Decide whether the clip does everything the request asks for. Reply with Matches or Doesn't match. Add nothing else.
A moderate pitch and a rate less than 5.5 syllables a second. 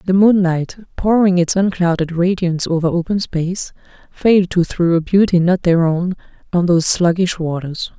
Matches